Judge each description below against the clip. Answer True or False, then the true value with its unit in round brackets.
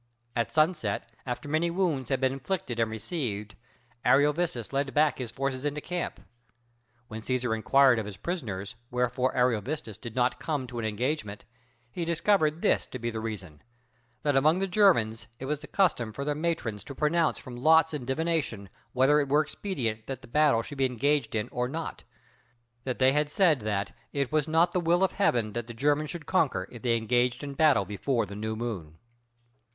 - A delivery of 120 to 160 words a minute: False (190 wpm)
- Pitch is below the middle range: True (130 Hz)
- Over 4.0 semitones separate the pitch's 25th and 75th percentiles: True (5.1 semitones)